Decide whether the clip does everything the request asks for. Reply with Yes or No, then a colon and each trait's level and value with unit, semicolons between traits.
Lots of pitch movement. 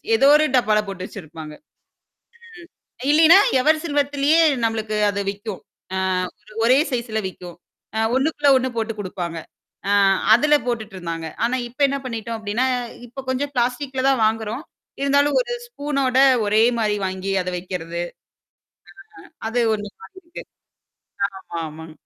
Yes: wide, 5.8 semitones